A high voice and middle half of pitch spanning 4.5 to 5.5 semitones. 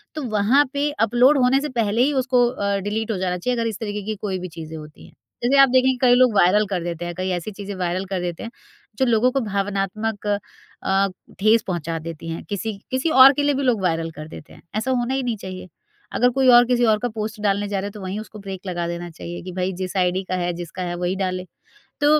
Yes: high, 205 Hz; average, 5.0 semitones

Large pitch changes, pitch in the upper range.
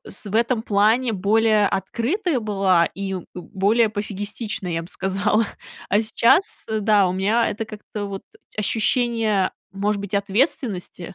No: narrow, 2.5 semitones; high, 210 Hz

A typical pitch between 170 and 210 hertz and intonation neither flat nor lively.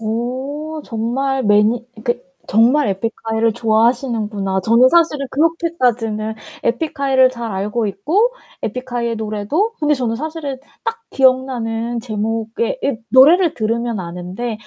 No: high, 240 Hz; average, 3.9 semitones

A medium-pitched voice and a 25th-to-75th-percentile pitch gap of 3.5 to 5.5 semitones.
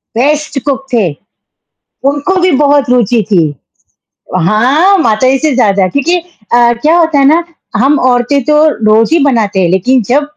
No: very high, 270 Hz; average, 4.5 semitones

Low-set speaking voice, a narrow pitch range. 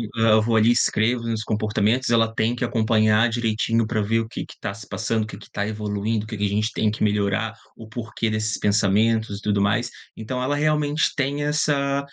Yes: low, 110 Hz; narrow, 1.9 semitones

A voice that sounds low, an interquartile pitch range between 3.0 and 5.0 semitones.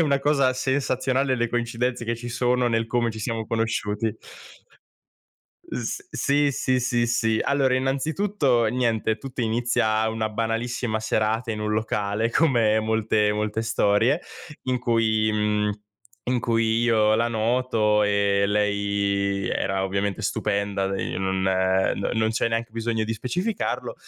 No: low, 115 Hz; narrow, 2.5 semitones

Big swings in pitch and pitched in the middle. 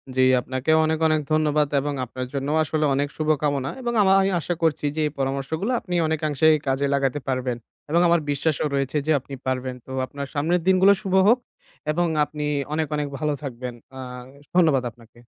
No: average, 2.9 semitones; medium, 150 Hz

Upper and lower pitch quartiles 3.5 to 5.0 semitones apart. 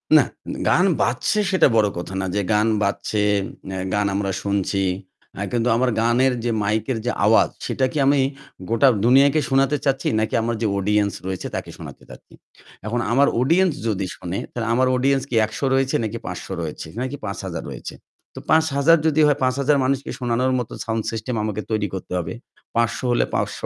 Yes: average, 4.4 semitones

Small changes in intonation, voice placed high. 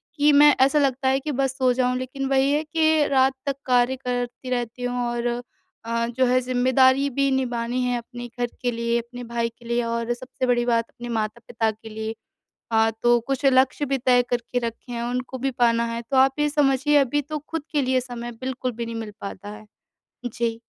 Yes: narrow, 2.2 semitones; high, 245 Hz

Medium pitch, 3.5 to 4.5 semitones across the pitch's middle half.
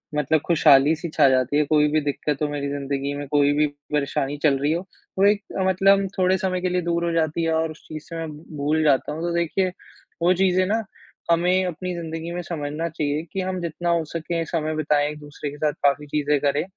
No: medium, 155 Hz; average, 2.8 semitones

